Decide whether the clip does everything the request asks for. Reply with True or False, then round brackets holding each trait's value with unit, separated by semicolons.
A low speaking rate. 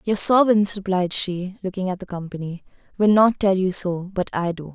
False (200 wpm)